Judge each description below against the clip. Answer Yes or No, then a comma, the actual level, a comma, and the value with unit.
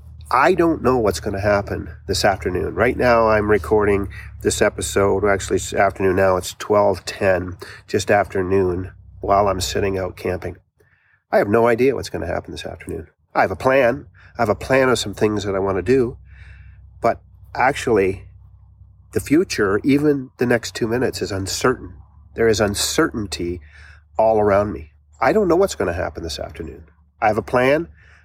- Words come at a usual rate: Yes, average, 185 wpm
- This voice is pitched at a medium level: No, very low, 95 Hz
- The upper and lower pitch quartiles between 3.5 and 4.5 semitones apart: No, average, 3.0 semitones